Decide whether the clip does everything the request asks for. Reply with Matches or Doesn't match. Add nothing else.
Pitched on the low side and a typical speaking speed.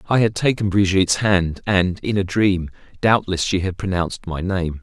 Matches